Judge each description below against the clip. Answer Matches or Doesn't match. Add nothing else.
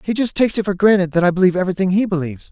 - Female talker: Doesn't match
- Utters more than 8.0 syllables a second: Matches